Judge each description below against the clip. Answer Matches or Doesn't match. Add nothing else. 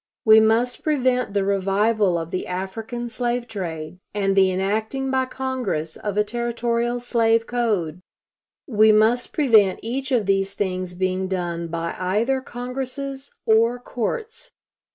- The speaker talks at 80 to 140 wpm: Matches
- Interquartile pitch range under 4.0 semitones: Doesn't match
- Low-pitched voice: Doesn't match